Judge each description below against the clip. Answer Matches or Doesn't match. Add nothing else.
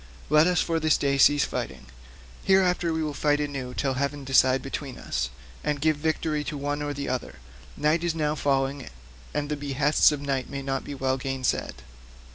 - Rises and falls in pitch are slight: Matches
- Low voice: Doesn't match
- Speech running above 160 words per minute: Matches